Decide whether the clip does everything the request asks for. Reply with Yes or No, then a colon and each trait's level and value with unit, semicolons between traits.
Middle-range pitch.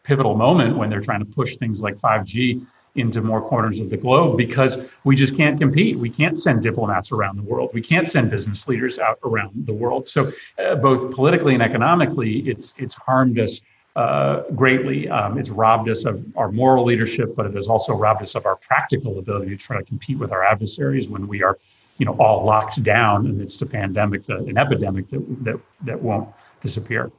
No: low, 120 Hz